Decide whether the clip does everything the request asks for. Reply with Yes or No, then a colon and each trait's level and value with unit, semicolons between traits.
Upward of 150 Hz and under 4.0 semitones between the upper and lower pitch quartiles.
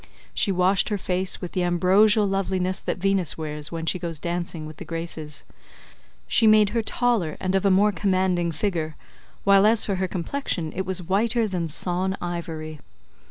Yes: medium, 185 Hz; average, 2.7 semitones